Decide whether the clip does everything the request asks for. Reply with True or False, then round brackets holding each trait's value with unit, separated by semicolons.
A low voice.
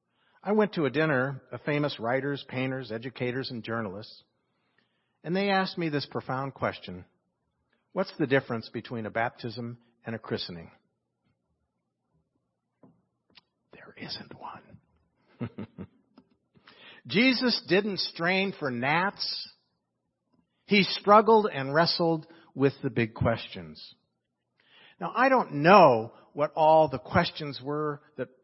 False (145 Hz)